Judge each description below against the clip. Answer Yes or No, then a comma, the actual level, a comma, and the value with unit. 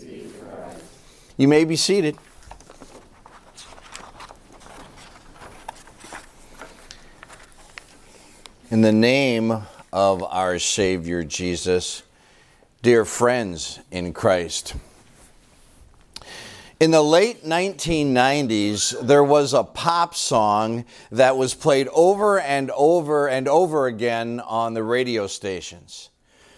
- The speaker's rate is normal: No, slow, 85 wpm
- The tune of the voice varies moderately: No, wide, 6.6 semitones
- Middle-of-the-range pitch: No, low, 120 Hz